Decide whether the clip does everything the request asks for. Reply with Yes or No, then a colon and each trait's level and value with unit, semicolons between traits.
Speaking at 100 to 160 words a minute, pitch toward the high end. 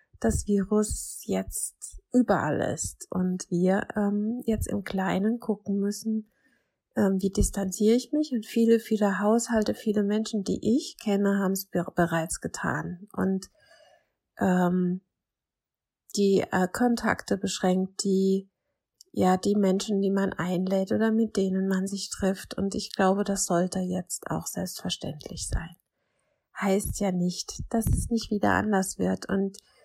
Yes: average, 140 wpm; high, 195 Hz